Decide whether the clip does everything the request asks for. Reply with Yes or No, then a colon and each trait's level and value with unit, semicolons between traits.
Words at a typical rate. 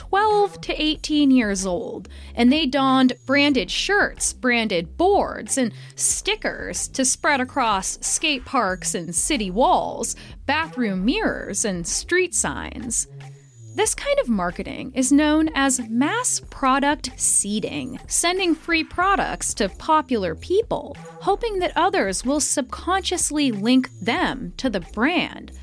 No: slow, 125 wpm